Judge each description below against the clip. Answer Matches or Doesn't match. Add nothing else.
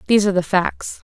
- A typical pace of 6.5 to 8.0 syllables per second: Matches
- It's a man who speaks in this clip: Doesn't match